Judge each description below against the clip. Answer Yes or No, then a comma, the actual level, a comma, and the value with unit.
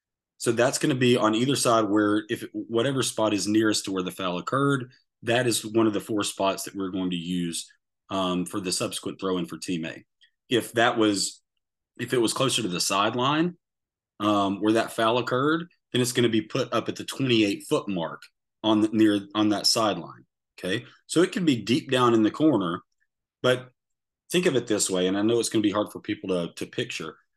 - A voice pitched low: Yes, low, 110 Hz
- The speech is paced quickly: Yes, fast, 225 wpm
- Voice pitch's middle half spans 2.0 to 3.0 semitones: No, average, 3.7 semitones